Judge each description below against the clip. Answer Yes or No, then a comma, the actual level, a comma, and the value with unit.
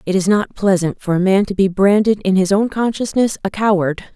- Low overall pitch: No, high, 200 Hz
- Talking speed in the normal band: No, fast, 230 wpm